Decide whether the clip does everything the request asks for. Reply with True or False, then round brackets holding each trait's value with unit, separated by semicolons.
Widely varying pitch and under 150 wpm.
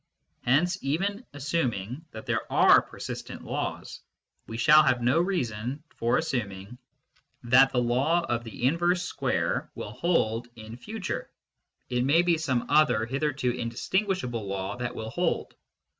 True (6.1 semitones; 140 wpm)